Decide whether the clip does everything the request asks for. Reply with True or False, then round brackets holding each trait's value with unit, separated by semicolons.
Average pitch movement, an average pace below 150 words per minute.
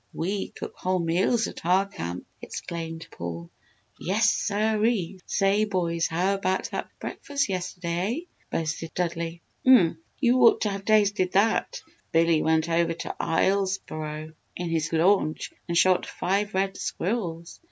True (3.4 semitones; 140 wpm)